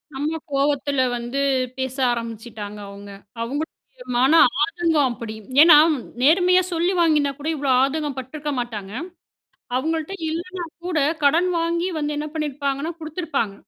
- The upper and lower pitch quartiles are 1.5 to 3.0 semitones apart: No, average, 4.1 semitones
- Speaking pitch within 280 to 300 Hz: Yes, very high, 290 Hz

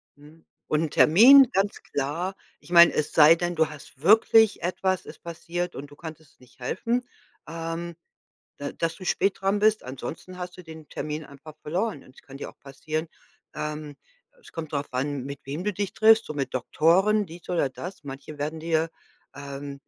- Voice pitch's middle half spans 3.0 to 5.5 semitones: Yes, average, 4.0 semitones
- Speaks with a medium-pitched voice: Yes, medium, 160 Hz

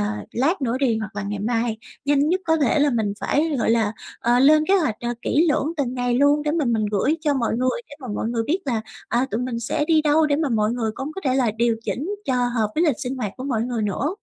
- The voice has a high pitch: Yes, very high, 255 Hz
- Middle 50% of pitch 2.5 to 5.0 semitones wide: Yes, average, 4.4 semitones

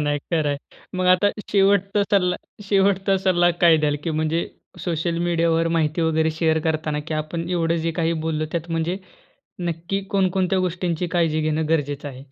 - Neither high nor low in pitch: Yes, medium, 165 Hz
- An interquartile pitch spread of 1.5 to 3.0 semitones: Yes, narrow, 2.5 semitones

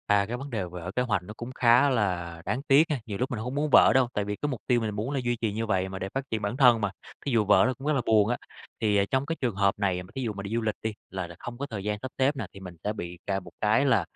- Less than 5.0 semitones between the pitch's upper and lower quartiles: Yes, average, 4.2 semitones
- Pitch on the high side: No, low, 110 Hz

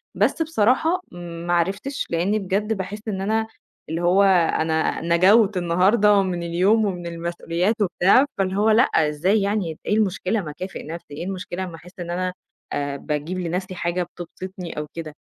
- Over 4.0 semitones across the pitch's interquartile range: No, average, 3.1 semitones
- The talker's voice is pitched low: No, medium, 185 Hz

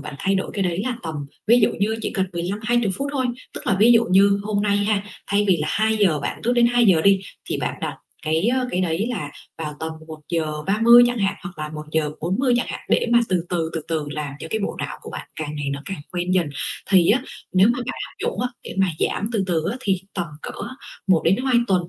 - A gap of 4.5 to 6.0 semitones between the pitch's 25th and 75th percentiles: Yes, average, 5.2 semitones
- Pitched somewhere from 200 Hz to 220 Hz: No, high, 190 Hz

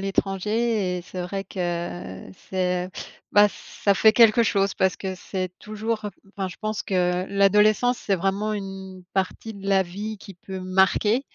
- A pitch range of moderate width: No, narrow, 2.3 semitones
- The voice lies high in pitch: Yes, high, 195 Hz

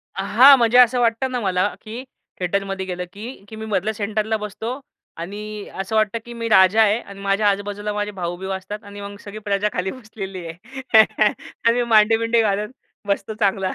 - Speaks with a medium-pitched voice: No, high, 210 Hz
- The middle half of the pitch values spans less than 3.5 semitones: Yes, narrow, 2.5 semitones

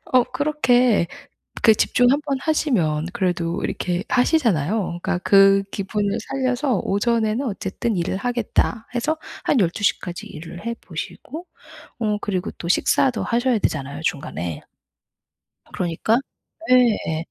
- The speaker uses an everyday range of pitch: No, wide, 5.9 semitones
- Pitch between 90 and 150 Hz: No, high, 215 Hz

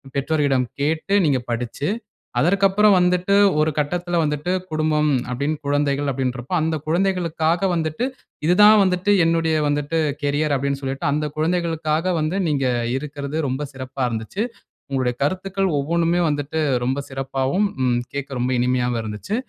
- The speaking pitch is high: No, medium, 150 Hz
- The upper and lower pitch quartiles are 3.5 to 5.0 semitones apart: Yes, average, 4.0 semitones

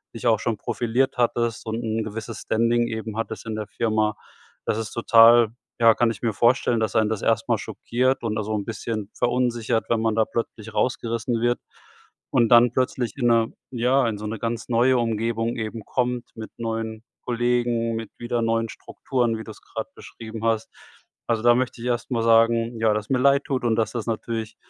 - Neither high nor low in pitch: No, low, 115 Hz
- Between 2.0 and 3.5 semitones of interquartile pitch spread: No, narrow, 1.3 semitones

